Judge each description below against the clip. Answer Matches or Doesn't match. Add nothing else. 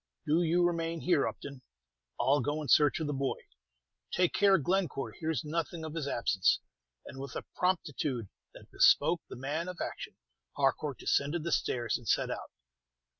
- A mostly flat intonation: Doesn't match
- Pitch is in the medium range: Matches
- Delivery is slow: Doesn't match